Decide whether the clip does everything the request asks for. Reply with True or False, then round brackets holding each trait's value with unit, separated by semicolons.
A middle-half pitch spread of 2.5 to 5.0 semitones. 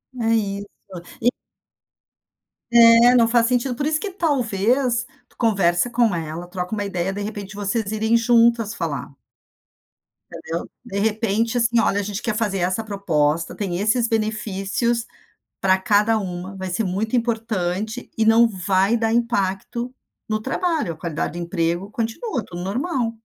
True (3.6 semitones)